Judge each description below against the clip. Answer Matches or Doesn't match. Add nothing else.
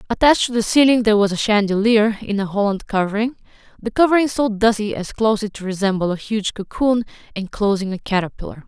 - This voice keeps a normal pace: Matches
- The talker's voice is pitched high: Matches